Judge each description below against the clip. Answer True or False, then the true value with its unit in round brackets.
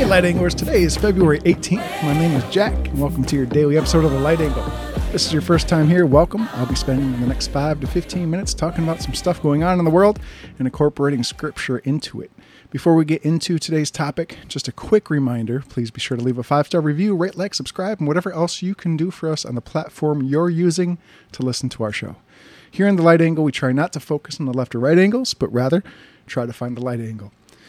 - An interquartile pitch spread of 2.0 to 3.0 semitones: False (4.8 semitones)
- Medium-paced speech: False (250 wpm)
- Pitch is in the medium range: True (155 Hz)